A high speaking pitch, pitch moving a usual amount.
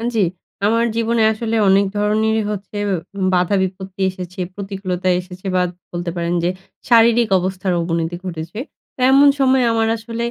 Yes: high, 195 Hz; average, 3.7 semitones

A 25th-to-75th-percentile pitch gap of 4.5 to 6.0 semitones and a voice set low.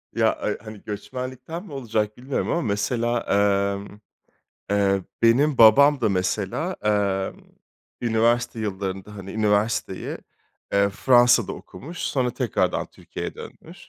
No: average, 3.6 semitones; low, 110 Hz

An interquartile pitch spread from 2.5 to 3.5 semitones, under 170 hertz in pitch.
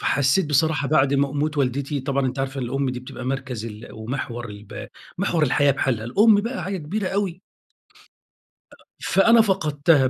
No: average, 4.3 semitones; medium, 140 Hz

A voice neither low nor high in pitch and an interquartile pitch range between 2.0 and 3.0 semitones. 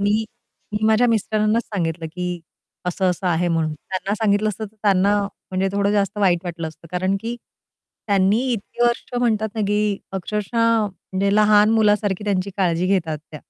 No: high, 200 Hz; average, 2.7 semitones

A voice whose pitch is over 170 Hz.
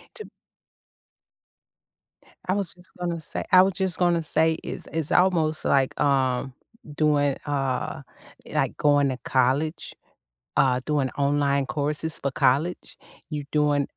No: medium, 150 Hz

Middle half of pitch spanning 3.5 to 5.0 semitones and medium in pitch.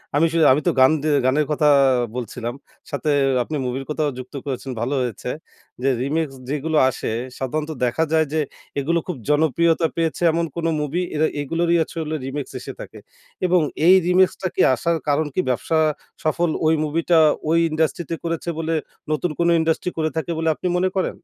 No: average, 2.8 semitones; medium, 155 Hz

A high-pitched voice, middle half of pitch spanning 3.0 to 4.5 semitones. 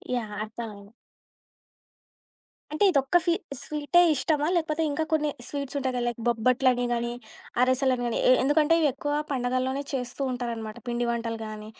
Yes: very high, 255 Hz; average, 3.5 semitones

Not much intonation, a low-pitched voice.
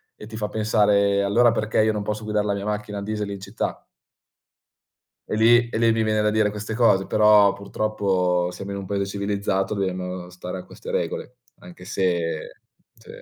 Yes: narrow, 1.8 semitones; low, 105 Hz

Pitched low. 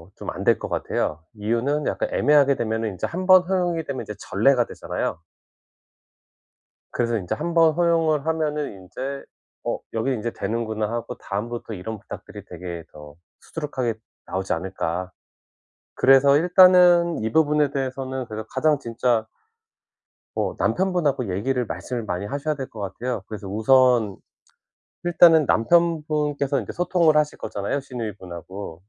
Yes: low, 130 Hz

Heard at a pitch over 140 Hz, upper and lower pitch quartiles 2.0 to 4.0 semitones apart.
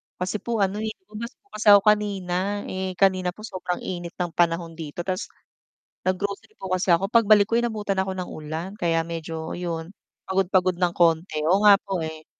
Yes: medium, 185 Hz; average, 3.0 semitones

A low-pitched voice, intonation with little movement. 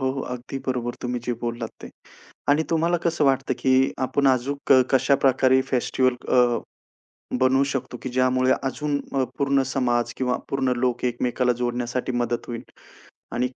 Yes: low, 130 Hz; narrow, 1.7 semitones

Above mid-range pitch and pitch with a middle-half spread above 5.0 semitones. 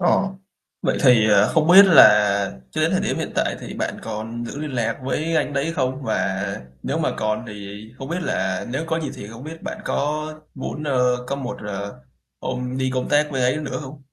No: low, 130 Hz; wide, 5.6 semitones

